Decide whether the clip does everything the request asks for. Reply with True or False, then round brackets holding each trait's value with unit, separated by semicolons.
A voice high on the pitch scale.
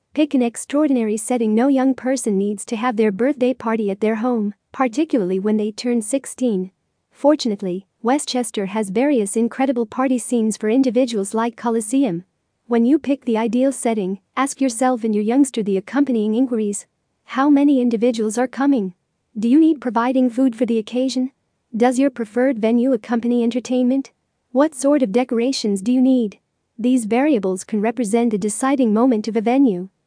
True (245 Hz)